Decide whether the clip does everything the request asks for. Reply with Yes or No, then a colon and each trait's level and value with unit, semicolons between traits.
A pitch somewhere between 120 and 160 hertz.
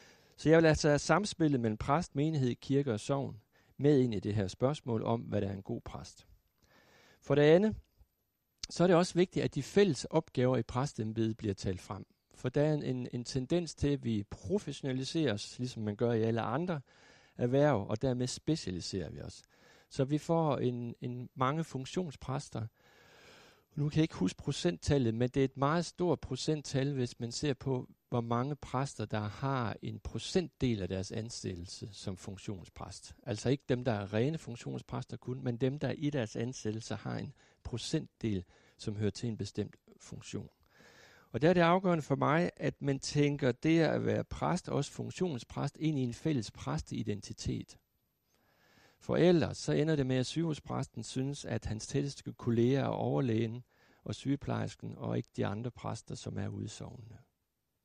Yes: low, 125 Hz